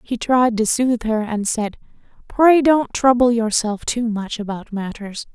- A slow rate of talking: No, average, 170 wpm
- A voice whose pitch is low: No, high, 230 Hz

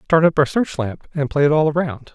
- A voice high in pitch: No, medium, 150 Hz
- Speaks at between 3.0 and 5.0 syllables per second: No, 5.5 syllables/s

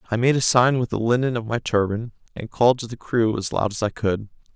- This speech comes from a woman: No, male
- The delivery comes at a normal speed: No, fast, 265 wpm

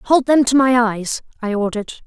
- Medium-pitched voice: No, high, 240 Hz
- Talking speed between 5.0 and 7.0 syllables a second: Yes, 5.1 syllables/s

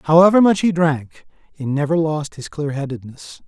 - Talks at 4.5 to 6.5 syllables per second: Yes, 5.1 syllables/s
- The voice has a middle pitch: Yes, medium, 155 Hz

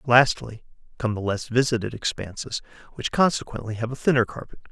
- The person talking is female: No, male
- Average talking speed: Yes, average, 155 wpm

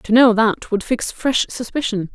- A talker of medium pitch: No, high, 225 Hz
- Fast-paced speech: No, average, 195 wpm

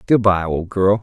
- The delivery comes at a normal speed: Yes, average, 175 wpm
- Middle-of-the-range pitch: No, low, 100 Hz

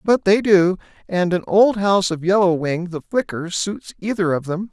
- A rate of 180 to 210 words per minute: Yes, fast, 205 wpm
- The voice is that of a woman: No, male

